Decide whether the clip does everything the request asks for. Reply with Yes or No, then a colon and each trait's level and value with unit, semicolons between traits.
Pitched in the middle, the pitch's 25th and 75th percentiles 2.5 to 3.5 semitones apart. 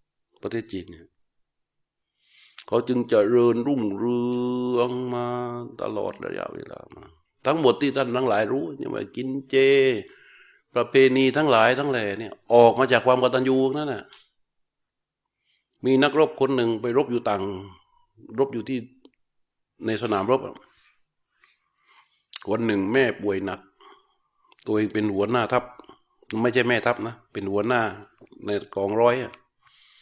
No: low, 125 Hz; average, 3.1 semitones